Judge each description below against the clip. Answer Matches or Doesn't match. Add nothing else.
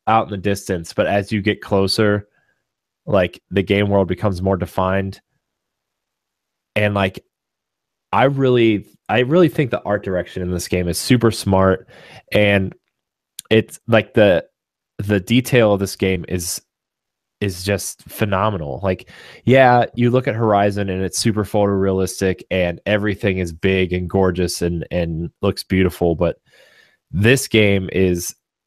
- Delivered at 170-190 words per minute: Doesn't match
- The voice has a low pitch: Matches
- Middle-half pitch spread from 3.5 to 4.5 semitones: Doesn't match